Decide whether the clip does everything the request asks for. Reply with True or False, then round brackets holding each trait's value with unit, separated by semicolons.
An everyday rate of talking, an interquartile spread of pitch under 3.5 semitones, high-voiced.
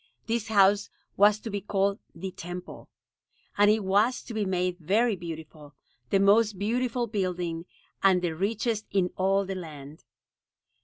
True (150 wpm; 2.9 semitones; 195 Hz)